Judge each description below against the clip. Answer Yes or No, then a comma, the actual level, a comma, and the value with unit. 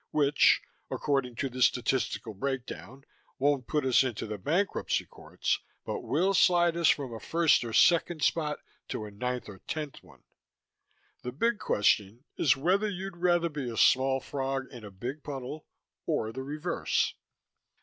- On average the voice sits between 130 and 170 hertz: Yes, low, 135 Hz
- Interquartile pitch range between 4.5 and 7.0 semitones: Yes, average, 4.8 semitones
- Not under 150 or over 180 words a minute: Yes, average, 160 wpm